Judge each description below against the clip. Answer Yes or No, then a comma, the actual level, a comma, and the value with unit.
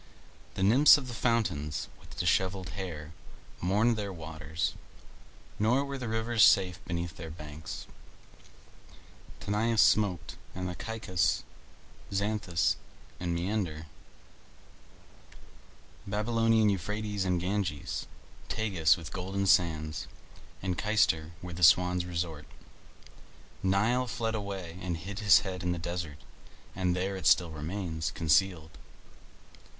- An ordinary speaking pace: No, slow, 115 wpm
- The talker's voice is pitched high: No, very low, 90 Hz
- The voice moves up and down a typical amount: Yes, average, 4.0 semitones